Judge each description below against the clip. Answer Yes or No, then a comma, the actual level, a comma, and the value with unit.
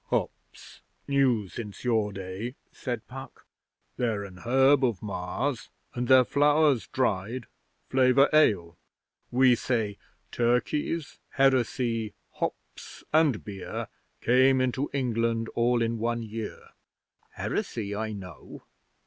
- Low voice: Yes, low, 120 Hz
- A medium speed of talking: No, slow, 110 wpm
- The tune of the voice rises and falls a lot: No, average, 3.5 semitones